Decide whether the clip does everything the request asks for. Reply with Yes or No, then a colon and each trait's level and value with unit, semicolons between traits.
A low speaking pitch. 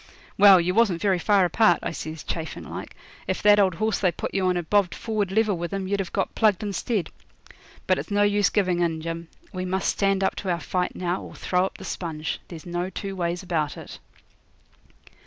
No: medium, 185 Hz